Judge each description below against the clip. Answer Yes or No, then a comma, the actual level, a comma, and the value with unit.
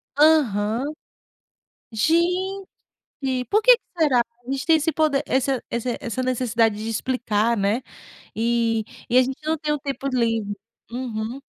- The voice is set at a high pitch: Yes, very high, 255 Hz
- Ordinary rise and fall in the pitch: Yes, average, 4.8 semitones